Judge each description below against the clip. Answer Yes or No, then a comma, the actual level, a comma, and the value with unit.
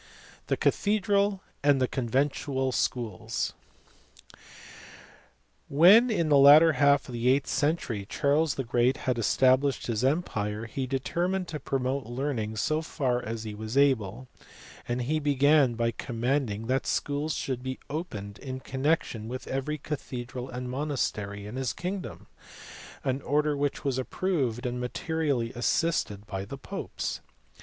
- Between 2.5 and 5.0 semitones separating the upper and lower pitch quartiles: Yes, average, 3.7 semitones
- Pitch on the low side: Yes, low, 130 Hz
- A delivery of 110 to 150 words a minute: Yes, slow, 135 wpm